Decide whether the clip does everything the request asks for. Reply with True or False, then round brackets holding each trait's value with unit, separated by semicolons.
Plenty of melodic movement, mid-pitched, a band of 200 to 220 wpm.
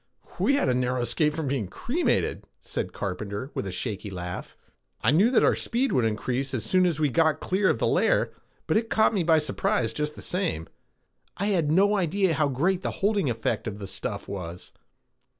True (8.9 semitones; 150 Hz; 205 wpm)